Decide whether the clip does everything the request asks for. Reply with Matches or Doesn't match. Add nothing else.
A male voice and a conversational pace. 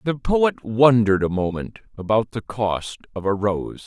Matches